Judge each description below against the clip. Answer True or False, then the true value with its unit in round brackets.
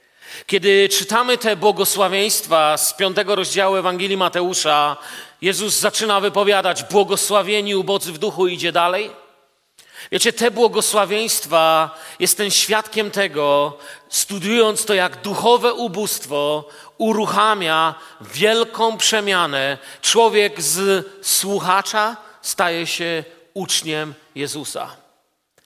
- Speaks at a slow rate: True (90 wpm)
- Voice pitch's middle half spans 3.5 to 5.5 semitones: True (4.1 semitones)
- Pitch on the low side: False (195 Hz)